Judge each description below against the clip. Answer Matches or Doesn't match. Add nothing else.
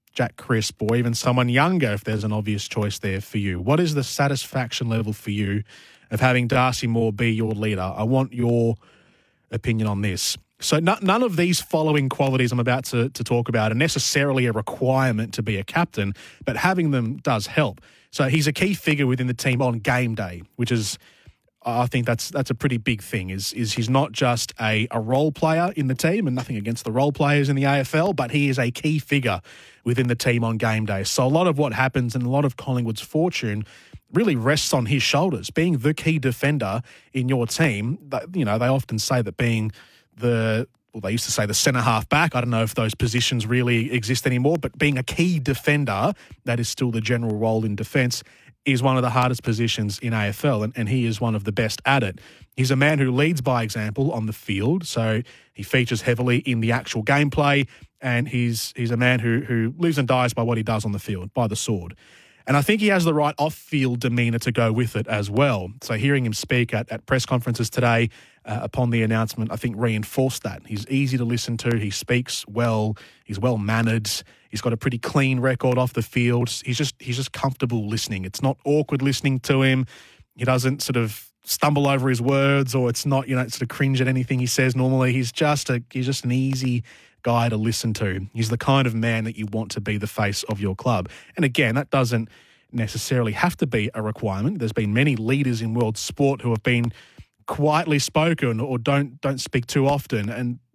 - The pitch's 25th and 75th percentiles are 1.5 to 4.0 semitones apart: Matches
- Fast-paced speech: Matches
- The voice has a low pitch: Matches